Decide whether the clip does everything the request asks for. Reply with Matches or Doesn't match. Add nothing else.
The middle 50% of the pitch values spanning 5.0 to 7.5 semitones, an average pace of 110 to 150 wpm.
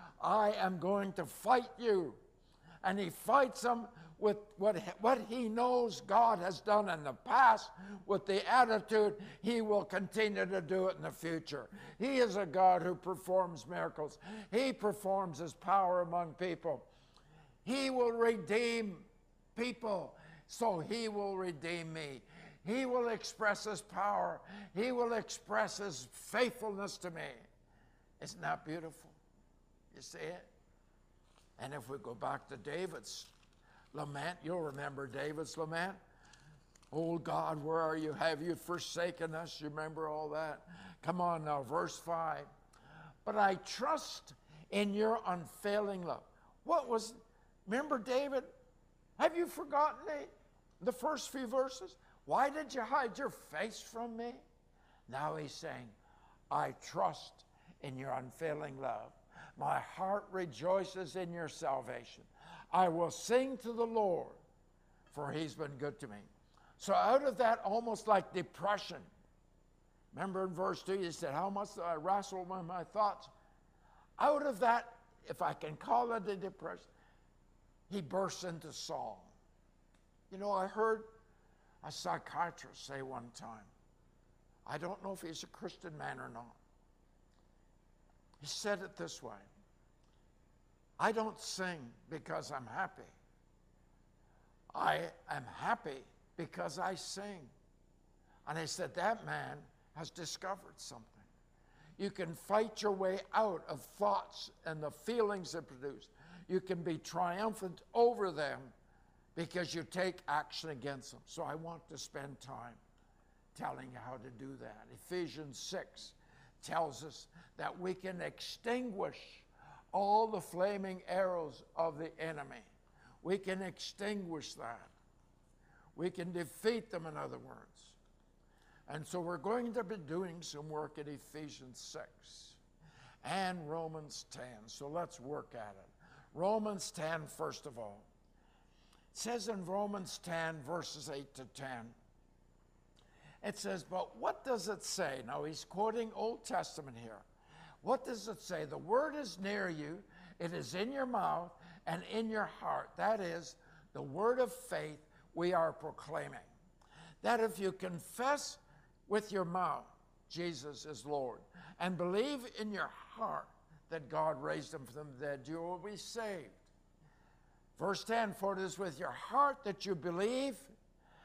Matches